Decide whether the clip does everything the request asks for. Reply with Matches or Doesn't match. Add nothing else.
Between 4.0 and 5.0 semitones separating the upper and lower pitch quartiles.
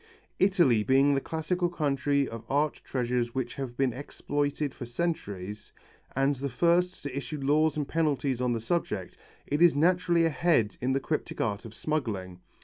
Matches